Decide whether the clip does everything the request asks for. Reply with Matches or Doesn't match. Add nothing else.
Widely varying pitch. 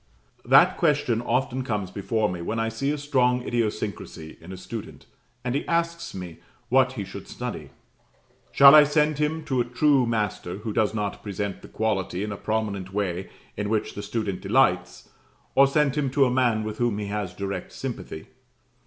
Doesn't match